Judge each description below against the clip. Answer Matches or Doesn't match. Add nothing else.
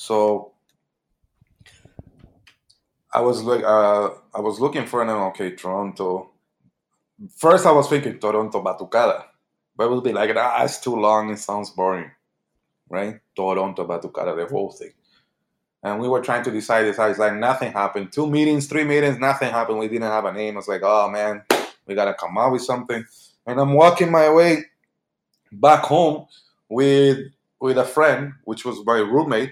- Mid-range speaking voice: Doesn't match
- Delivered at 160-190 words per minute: Matches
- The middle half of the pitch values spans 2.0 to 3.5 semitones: Doesn't match